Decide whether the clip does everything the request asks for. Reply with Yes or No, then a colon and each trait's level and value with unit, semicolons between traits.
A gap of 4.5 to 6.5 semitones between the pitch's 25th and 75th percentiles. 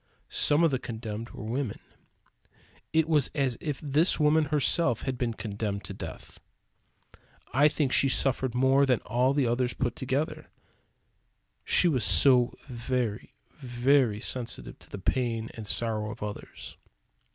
No: average, 3.4 semitones